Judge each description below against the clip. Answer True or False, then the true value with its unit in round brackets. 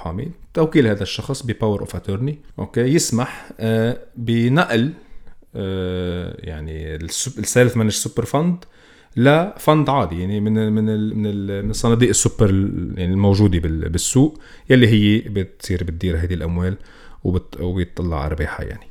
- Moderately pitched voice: False (105 Hz)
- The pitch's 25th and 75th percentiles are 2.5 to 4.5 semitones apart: False (5.3 semitones)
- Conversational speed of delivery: True (115 wpm)